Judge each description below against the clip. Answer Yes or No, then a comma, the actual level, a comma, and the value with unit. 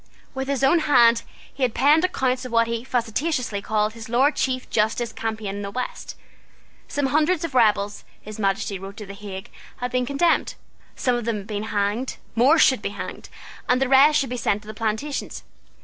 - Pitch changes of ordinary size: Yes, average, 4.1 semitones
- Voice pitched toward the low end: No, high, 240 Hz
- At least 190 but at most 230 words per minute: Yes, average, 200 wpm